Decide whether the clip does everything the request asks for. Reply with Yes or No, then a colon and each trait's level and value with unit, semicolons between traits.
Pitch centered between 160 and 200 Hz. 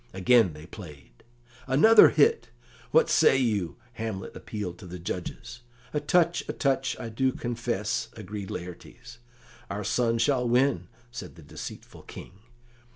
No: low, 115 Hz